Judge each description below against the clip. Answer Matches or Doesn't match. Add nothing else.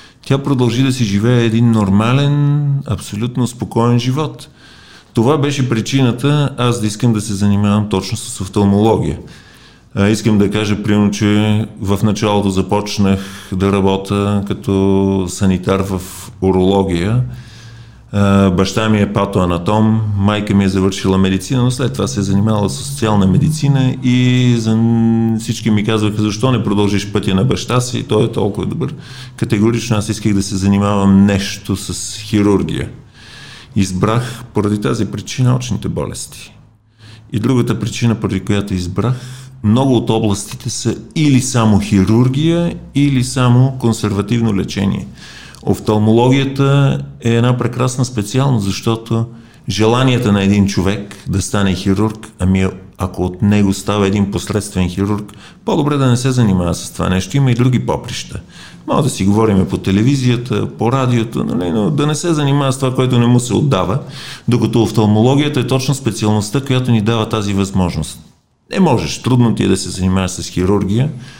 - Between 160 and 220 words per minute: Doesn't match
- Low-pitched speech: Matches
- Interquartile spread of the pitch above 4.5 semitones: Doesn't match